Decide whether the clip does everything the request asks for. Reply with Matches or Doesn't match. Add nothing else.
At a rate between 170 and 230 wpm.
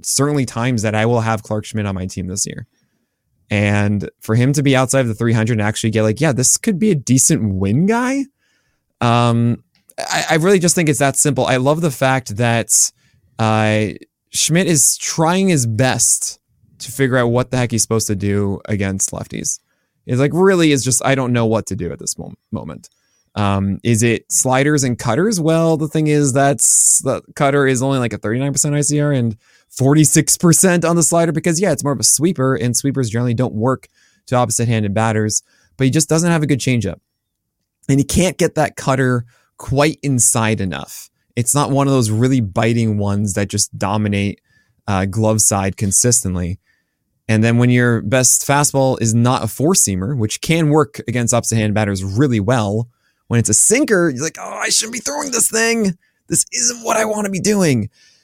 Matches